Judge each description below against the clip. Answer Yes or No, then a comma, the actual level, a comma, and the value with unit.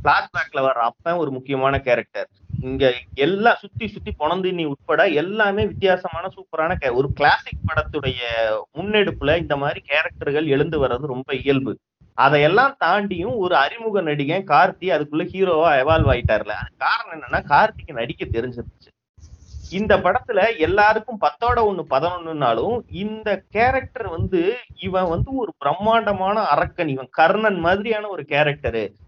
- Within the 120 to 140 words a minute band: Yes, average, 125 wpm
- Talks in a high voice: No, medium, 160 Hz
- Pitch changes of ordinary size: No, wide, 6.8 semitones